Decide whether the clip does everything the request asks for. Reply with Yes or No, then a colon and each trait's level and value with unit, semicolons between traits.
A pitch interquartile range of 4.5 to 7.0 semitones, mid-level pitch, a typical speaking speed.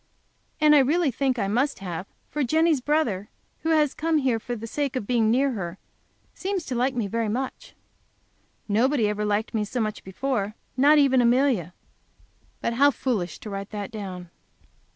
No: average, 5.1 semitones; high, 245 Hz; average, 175 wpm